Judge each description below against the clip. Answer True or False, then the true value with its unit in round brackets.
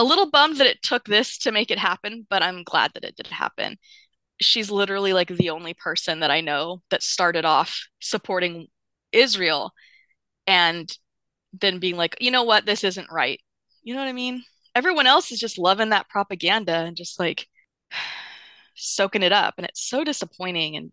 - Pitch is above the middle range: True (195 Hz)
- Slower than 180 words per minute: False (185 wpm)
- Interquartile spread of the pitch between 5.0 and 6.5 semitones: True (5.5 semitones)